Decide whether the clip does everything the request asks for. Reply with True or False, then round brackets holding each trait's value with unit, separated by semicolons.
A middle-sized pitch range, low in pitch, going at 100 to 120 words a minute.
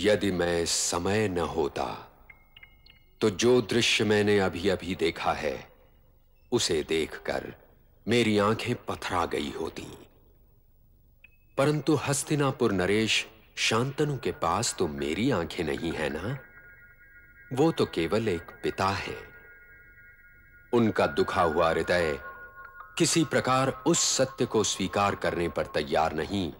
False (7.9 semitones; 130 Hz; 115 wpm)